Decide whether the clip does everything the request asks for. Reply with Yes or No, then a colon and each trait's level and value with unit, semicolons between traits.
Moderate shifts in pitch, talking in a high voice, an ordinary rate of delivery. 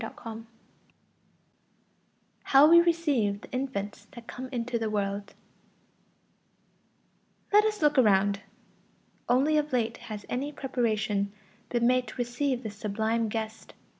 No: average, 4.2 semitones; high, 240 Hz; slow, 115 wpm